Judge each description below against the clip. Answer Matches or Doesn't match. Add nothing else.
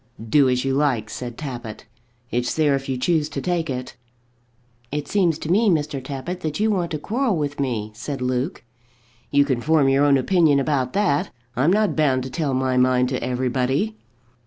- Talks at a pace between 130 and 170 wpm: Doesn't match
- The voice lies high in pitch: Doesn't match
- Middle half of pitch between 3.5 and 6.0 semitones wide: Matches